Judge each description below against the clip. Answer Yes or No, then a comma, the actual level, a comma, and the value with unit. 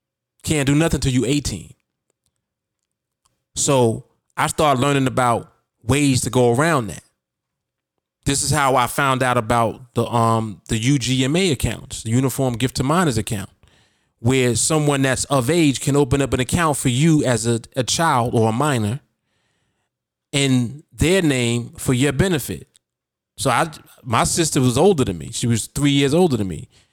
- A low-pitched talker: Yes, low, 130 Hz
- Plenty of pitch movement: No, average, 3.6 semitones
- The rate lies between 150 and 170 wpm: Yes, average, 165 wpm